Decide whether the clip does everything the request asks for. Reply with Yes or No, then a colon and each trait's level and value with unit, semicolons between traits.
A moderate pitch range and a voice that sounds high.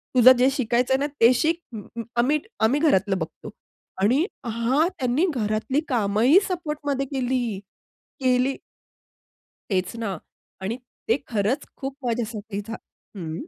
Yes: average, 4.1 semitones; high, 245 Hz